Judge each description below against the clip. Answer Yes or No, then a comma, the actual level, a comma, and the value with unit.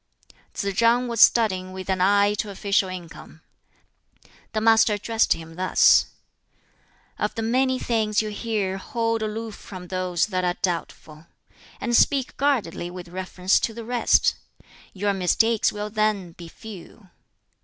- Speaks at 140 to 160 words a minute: Yes, average, 145 wpm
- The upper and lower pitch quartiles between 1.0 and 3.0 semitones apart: No, average, 3.5 semitones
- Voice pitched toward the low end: No, high, 205 Hz